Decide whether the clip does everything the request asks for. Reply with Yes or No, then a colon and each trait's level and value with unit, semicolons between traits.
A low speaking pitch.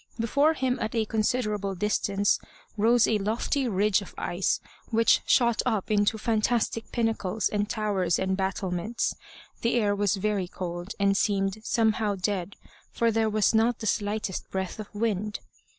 No: high, 210 Hz